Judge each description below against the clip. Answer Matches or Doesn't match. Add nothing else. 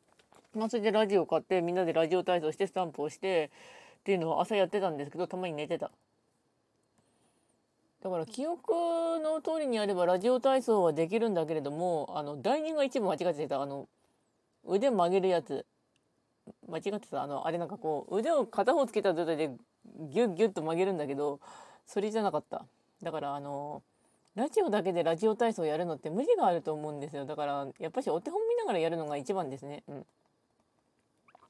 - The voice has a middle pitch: Matches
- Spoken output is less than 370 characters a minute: Doesn't match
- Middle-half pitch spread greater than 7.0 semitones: Doesn't match